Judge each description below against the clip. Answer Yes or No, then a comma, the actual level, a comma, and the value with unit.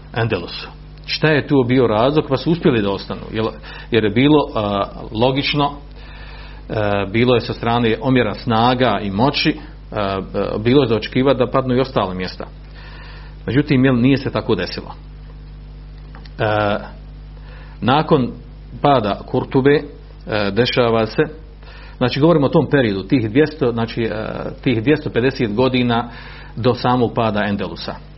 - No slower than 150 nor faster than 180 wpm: No, average, 135 wpm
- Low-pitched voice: Yes, low, 125 Hz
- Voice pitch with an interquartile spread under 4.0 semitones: No, average, 4.5 semitones